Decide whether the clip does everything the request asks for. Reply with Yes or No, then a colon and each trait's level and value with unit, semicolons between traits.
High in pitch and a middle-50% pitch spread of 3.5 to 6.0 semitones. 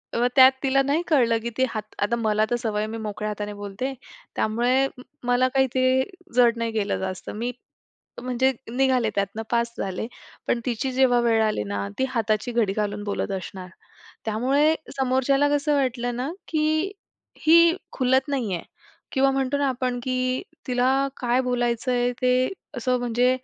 No: high, 245 Hz; average, 3.0 semitones